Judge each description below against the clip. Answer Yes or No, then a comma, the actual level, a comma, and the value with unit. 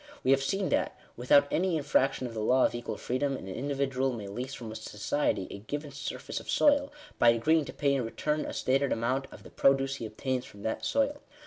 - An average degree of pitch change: Yes, average, 3.6 semitones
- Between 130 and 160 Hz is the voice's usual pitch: Yes, low, 135 Hz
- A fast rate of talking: Yes, fast, 215 wpm